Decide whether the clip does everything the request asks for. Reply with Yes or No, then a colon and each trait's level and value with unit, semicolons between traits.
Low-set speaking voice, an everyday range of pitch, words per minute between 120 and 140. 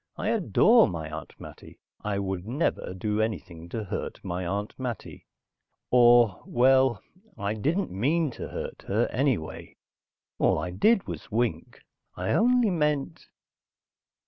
No: low, 110 Hz; wide, 7.1 semitones; slow, 135 wpm